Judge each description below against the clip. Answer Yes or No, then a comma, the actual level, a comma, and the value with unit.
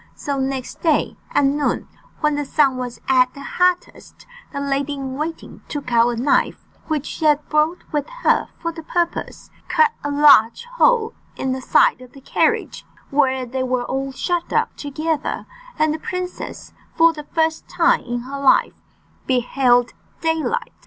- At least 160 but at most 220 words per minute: Yes, average, 165 wpm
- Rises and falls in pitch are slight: No, average, 3.6 semitones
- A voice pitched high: Yes, very high, 285 Hz